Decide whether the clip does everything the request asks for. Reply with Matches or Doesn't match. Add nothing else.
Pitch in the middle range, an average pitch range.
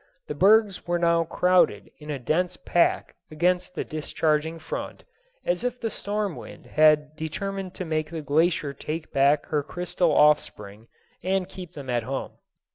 Matches